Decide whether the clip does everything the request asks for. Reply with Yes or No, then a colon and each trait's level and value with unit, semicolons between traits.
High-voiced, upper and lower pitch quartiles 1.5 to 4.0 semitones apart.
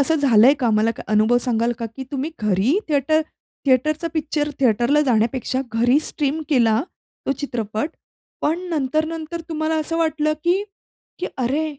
No: very high, 275 Hz; average, 4.8 semitones